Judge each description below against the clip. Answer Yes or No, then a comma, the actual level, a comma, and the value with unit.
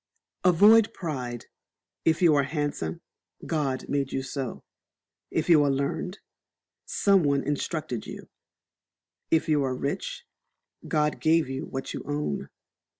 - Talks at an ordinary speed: No, slow, 130 wpm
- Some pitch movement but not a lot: Yes, average, 3.3 semitones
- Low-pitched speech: No, medium, 145 Hz